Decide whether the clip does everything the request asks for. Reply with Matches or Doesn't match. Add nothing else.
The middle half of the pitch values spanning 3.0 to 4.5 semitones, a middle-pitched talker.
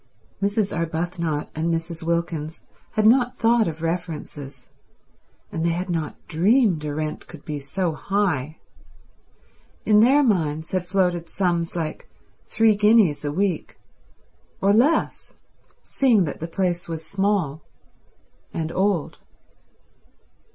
Matches